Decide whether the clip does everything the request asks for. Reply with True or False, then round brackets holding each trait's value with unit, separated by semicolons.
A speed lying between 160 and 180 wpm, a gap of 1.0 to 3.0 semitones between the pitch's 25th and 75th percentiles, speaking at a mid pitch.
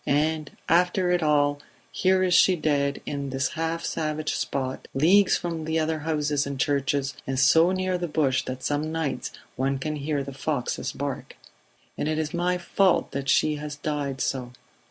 True (175 wpm; 2.7 semitones; 150 Hz)